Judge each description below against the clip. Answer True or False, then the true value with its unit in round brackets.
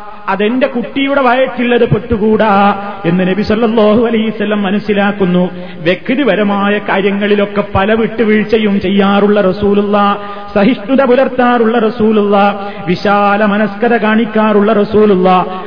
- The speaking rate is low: False (85 wpm)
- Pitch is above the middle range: True (205 Hz)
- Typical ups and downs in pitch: False (1.8 semitones)